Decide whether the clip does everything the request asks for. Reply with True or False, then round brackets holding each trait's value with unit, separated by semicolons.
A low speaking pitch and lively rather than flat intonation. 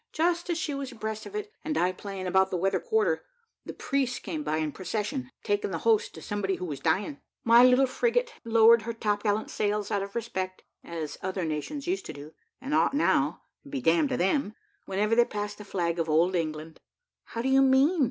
False (215 Hz; 6.5 semitones)